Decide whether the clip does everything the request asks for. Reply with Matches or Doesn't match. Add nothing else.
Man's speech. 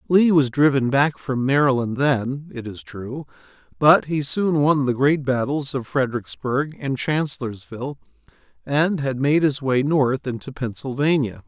Matches